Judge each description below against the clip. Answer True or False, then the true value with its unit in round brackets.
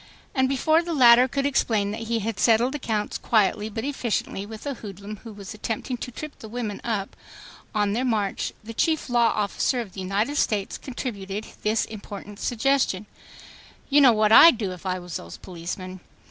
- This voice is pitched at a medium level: False (220 Hz)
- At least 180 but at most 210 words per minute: True (185 wpm)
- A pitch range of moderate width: True (3.6 semitones)